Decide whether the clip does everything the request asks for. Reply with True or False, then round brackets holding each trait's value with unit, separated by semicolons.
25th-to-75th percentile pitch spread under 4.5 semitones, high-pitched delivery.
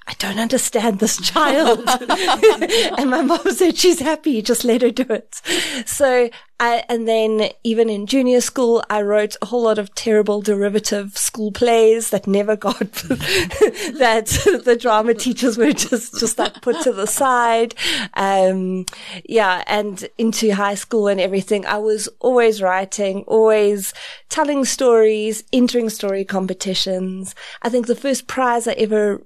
True (3.3 semitones; 230 Hz)